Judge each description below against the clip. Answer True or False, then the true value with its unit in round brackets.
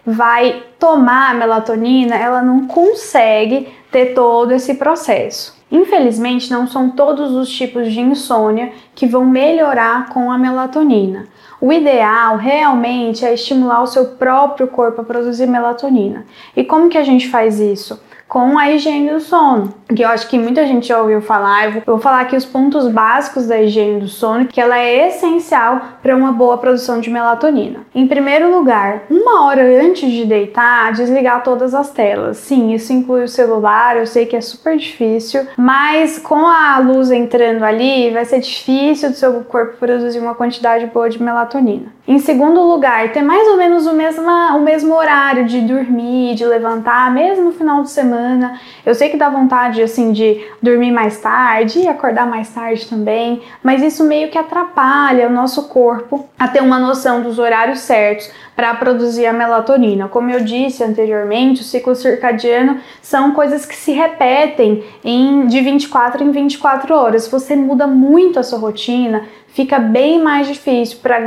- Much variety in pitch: False (3.1 semitones)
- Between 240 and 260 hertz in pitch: True (250 Hz)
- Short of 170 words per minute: False (175 wpm)